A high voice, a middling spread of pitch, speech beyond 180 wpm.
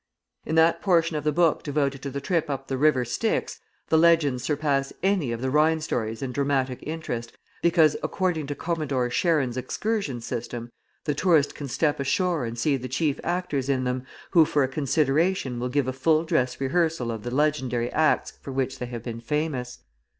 No: medium, 140 Hz; average, 3.9 semitones; average, 190 wpm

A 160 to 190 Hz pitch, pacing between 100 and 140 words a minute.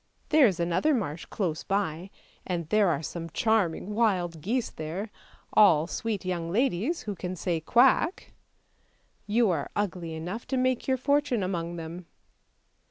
No: medium, 185 Hz; average, 150 wpm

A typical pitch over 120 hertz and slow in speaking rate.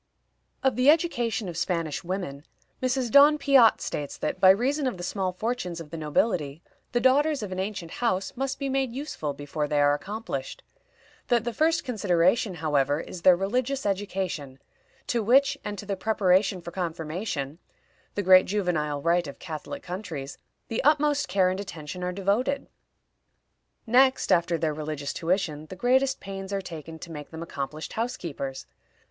No: medium, 185 Hz; average, 165 wpm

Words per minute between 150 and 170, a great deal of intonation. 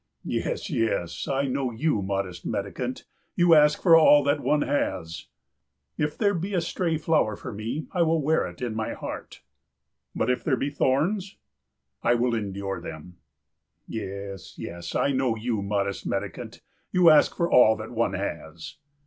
Yes: average, 165 wpm; wide, 7.5 semitones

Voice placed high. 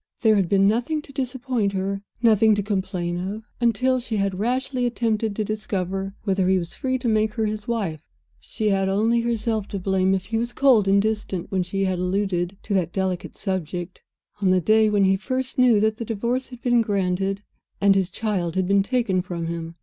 Yes: high, 205 Hz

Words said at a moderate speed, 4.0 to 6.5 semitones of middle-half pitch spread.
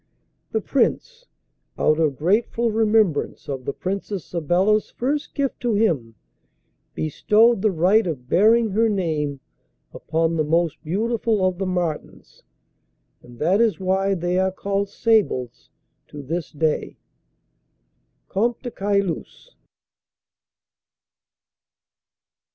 No: slow, 110 wpm; wide, 5.4 semitones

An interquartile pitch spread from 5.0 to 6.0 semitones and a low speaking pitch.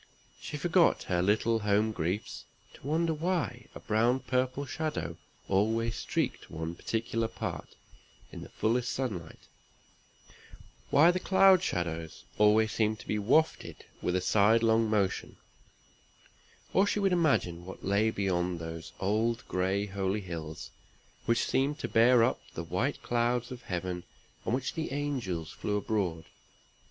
Yes: wide, 5.5 semitones; low, 110 Hz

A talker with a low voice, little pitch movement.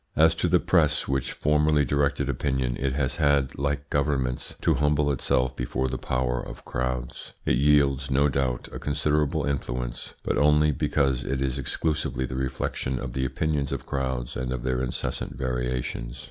Yes: very low, 65 Hz; narrow, 2.2 semitones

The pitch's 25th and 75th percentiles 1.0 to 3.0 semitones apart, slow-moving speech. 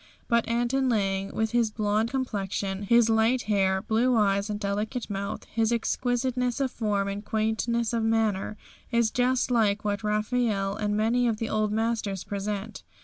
No: narrow, 2.4 semitones; average, 160 wpm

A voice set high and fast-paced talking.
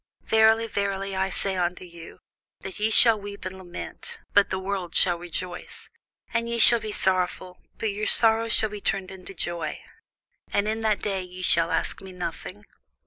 No: high, 195 Hz; average, 180 wpm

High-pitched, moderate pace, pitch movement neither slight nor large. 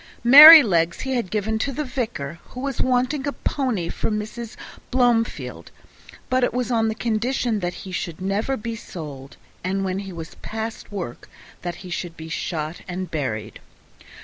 No: high, 215 Hz; average, 170 wpm; wide, 5.9 semitones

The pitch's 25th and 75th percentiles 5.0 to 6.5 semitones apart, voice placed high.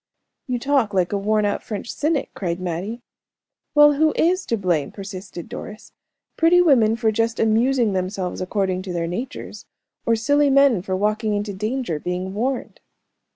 Yes: wide, 5.5 semitones; high, 215 Hz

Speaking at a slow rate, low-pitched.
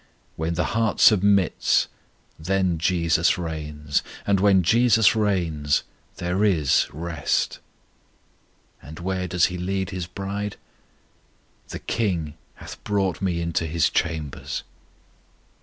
Yes: slow, 110 wpm; very low, 90 Hz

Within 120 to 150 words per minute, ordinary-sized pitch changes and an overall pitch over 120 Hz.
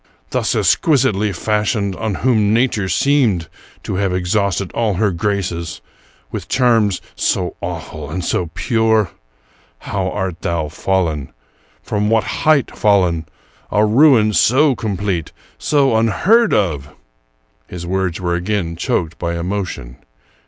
No: average, 140 wpm; average, 4.3 semitones; low, 100 Hz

